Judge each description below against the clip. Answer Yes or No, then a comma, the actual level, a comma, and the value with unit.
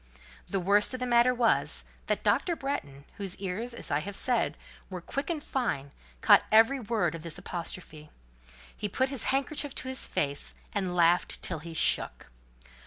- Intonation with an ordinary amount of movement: No, wide, 6.8 semitones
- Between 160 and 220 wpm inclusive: Yes, average, 175 wpm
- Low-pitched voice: No, high, 205 Hz